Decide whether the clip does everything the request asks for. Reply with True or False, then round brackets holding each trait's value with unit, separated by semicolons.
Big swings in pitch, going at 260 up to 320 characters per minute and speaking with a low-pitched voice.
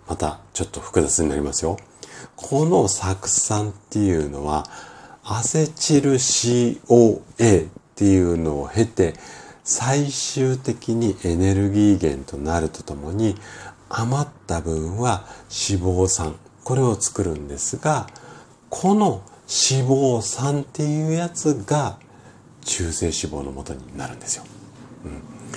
False (7.5 semitones; 240 characters per minute; 105 Hz)